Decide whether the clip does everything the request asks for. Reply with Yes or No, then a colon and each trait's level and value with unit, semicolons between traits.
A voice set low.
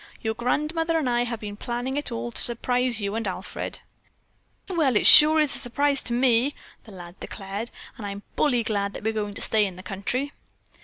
No: high, 235 Hz